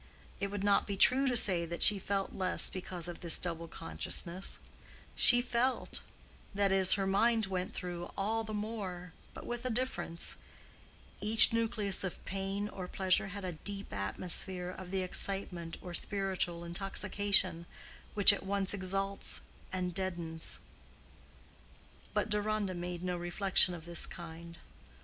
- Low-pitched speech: No, high, 190 Hz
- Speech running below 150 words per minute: Yes, average, 140 wpm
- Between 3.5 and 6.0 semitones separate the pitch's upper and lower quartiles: No, narrow, 2.5 semitones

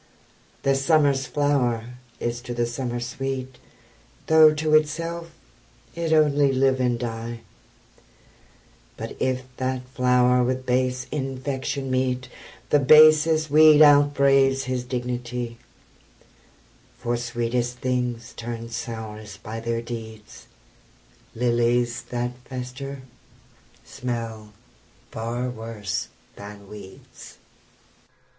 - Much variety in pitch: No, narrow, 2.5 semitones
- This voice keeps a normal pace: No, slow, 100 wpm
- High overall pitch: No, low, 125 Hz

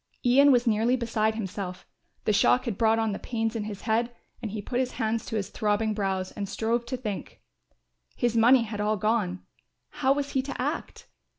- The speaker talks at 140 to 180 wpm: No, average, 200 wpm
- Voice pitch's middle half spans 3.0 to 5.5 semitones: No, narrow, 2.6 semitones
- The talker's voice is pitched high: Yes, high, 225 Hz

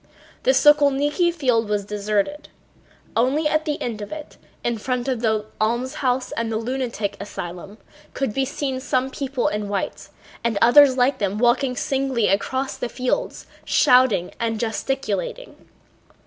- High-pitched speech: Yes, very high, 250 Hz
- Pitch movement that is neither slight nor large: Yes, average, 3.9 semitones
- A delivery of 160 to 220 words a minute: No, average, 145 wpm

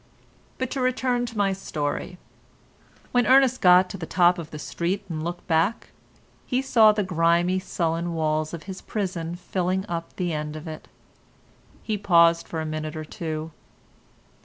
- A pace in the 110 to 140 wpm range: No, average, 165 wpm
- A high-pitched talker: No, medium, 175 Hz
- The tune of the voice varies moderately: Yes, average, 3.7 semitones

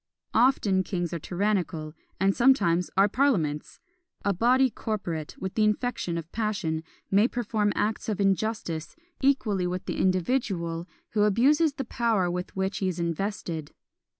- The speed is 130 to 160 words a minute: Yes, average, 145 wpm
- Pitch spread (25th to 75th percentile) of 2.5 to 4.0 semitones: No, average, 4.4 semitones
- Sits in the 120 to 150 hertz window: No, high, 195 Hz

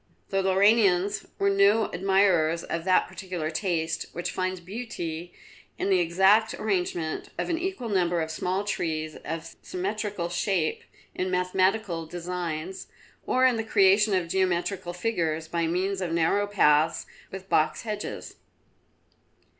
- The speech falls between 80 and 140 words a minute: Yes, slow, 135 wpm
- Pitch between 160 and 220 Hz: Yes, medium, 185 Hz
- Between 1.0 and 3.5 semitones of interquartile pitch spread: Yes, average, 2.9 semitones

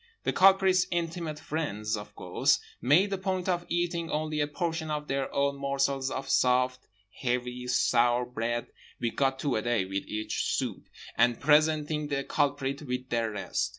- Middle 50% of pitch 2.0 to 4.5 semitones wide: Yes, average, 4.2 semitones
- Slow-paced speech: No, average, 165 wpm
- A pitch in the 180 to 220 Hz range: No, medium, 140 Hz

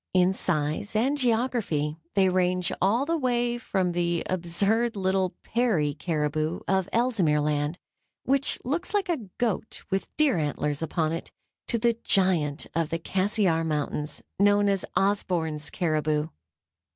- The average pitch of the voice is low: No, medium, 185 Hz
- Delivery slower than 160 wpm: Yes, average, 140 wpm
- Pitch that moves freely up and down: Yes, wide, 6.1 semitones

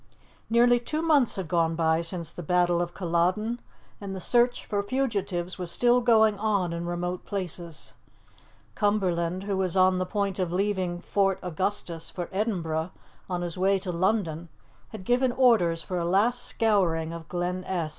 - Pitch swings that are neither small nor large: Yes, average, 3.3 semitones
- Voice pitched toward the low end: No, medium, 185 Hz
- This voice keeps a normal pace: Yes, average, 165 wpm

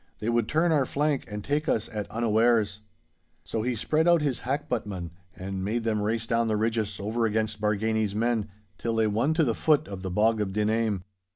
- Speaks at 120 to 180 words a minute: No, average, 200 wpm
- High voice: No, low, 110 Hz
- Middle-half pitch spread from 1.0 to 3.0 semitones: Yes, narrow, 2.5 semitones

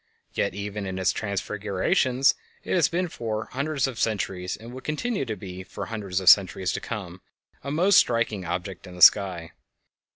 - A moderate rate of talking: Yes, average, 175 wpm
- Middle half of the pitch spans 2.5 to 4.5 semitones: No, wide, 5.5 semitones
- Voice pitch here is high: No, low, 105 Hz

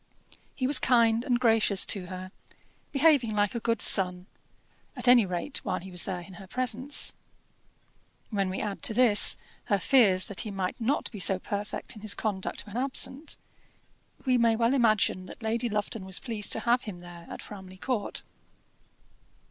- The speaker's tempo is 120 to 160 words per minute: No, average, 175 wpm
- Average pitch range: Yes, average, 4.1 semitones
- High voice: Yes, high, 215 Hz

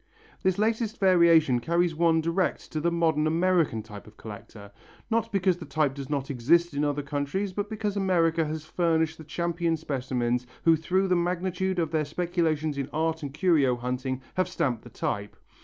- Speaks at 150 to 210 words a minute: Yes, average, 180 wpm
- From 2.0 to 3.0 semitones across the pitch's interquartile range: No, average, 4.0 semitones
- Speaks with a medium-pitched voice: Yes, medium, 160 Hz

